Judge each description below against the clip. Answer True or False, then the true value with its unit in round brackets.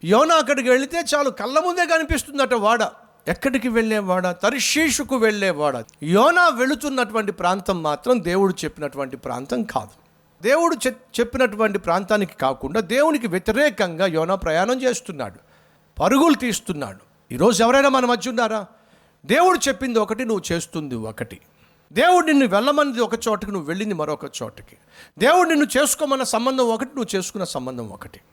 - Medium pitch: False (225 Hz)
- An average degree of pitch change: False (6.6 semitones)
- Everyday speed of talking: False (130 wpm)